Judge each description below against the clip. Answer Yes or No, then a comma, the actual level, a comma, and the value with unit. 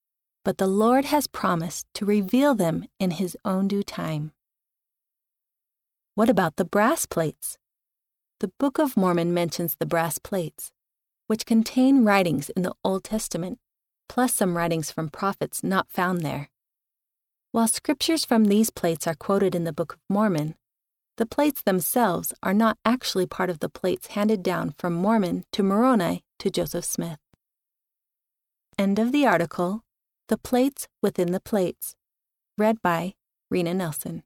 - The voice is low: No, high, 195 Hz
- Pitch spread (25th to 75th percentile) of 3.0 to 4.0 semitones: No, average, 4.5 semitones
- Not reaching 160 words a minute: Yes, average, 150 wpm